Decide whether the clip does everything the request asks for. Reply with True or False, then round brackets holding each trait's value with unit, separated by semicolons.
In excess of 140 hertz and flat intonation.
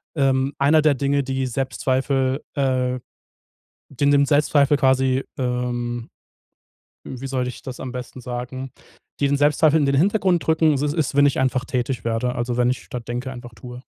False (130 Hz; 2.2 semitones)